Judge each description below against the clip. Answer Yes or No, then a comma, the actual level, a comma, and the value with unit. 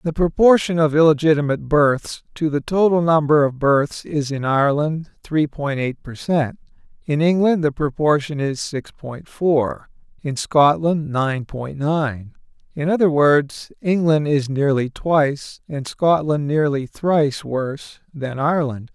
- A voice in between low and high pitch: Yes, medium, 150 Hz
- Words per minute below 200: Yes, average, 145 wpm